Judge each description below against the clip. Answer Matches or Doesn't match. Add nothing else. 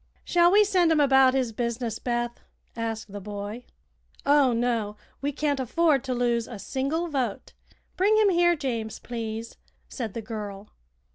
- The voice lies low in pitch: Doesn't match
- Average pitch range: Matches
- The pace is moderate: Matches